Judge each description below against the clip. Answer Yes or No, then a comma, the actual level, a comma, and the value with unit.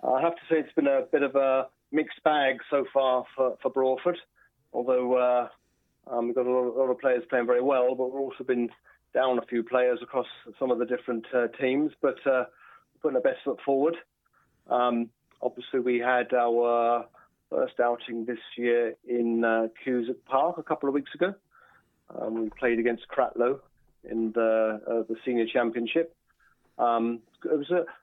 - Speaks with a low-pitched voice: Yes, low, 125 Hz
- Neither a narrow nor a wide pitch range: No, narrow, 2.2 semitones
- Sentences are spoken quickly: No, average, 185 wpm